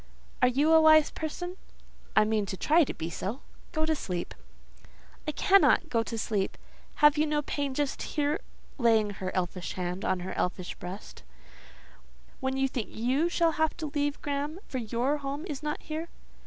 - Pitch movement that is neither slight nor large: No, wide, 6.2 semitones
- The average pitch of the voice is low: No, very high, 280 Hz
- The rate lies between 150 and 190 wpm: Yes, average, 180 wpm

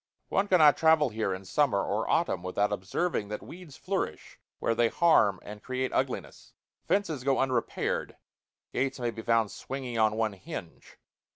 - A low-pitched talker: Yes, low, 120 Hz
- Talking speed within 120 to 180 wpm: Yes, average, 160 wpm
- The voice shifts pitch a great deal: Yes, wide, 5.9 semitones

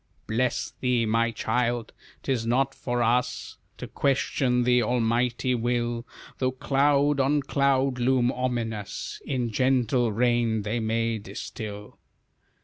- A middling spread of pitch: No, narrow, 2.0 semitones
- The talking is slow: Yes, slow, 120 wpm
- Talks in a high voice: No, low, 120 Hz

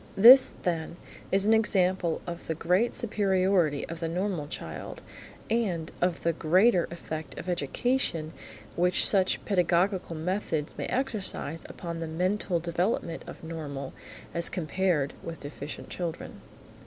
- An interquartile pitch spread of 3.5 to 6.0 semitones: No, average, 2.9 semitones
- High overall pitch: No, medium, 175 Hz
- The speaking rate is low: Yes, slow, 130 wpm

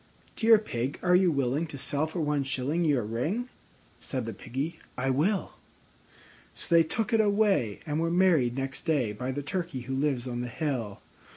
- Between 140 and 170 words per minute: No, average, 185 wpm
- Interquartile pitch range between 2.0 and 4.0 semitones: No, average, 5.3 semitones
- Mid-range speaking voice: Yes, medium, 145 Hz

